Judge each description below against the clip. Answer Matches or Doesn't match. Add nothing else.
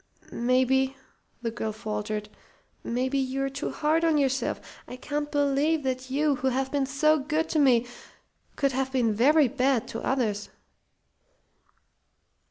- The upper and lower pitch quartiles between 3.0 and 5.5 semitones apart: Doesn't match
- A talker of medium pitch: Doesn't match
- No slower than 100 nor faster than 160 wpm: Matches